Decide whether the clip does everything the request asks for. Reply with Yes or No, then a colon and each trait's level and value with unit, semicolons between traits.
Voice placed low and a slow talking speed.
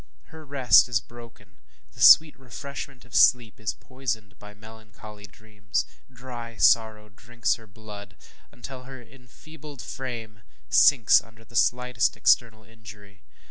Yes: low, 115 Hz; slow, 130 wpm